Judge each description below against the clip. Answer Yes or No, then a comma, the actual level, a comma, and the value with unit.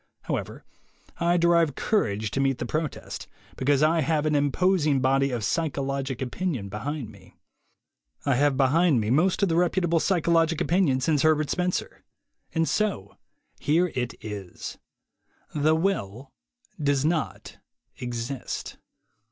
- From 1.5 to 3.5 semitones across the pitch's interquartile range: No, average, 4.3 semitones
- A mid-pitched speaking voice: Yes, medium, 145 Hz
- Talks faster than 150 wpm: No, slow, 135 wpm